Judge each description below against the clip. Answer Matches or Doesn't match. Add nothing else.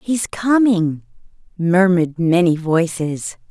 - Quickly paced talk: Doesn't match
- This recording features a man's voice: Doesn't match